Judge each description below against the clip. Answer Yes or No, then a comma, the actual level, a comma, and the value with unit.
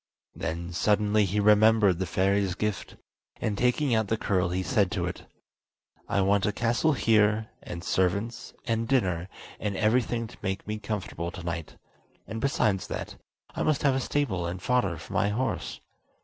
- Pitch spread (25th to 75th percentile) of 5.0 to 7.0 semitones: No, average, 3.4 semitones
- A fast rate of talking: No, average, 165 wpm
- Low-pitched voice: Yes, low, 105 Hz